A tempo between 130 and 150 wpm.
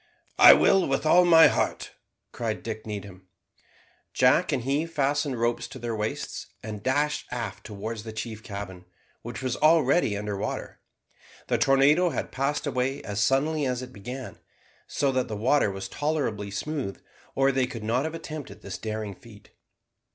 No: average, 165 wpm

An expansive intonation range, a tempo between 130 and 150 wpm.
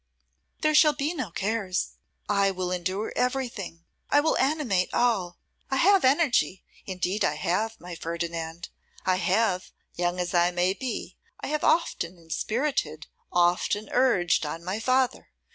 Yes: wide, 6.4 semitones; average, 145 wpm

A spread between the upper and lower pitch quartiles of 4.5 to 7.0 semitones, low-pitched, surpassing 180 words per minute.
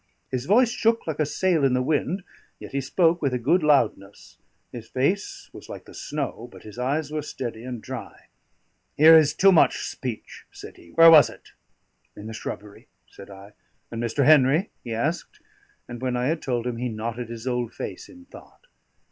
Yes: average, 5.2 semitones; low, 130 Hz; average, 195 wpm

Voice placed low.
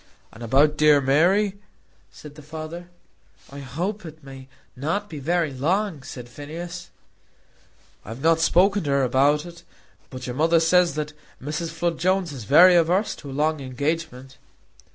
No: medium, 155 Hz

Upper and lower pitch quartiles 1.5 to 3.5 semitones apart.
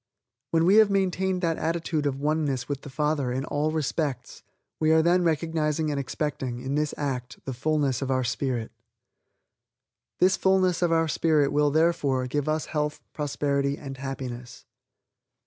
Yes: average, 3.1 semitones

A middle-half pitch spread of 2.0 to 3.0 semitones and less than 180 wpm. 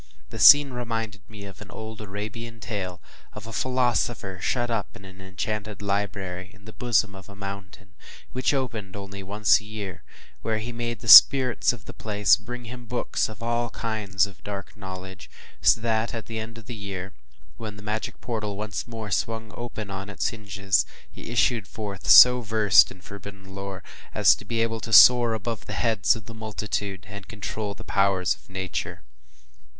No: average, 2.7 semitones; average, 185 wpm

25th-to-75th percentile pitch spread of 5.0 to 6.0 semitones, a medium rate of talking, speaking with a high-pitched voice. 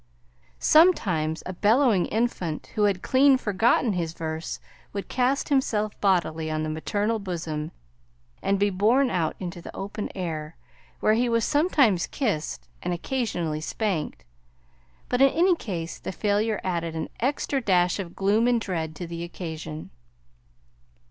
Yes: wide, 5.6 semitones; average, 145 wpm; high, 195 Hz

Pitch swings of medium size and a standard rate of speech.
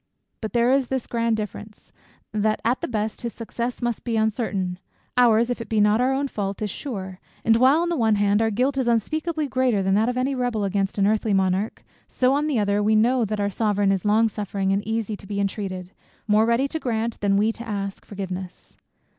No: average, 3.3 semitones; fast, 220 wpm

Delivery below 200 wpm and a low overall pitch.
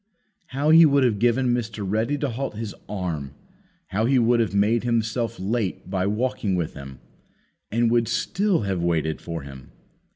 Yes: average, 170 wpm; low, 110 Hz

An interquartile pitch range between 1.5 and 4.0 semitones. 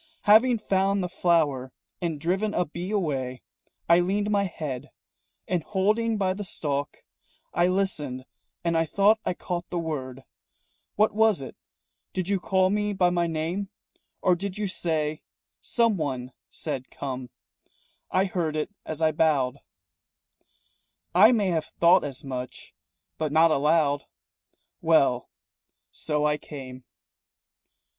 No: average, 4.8 semitones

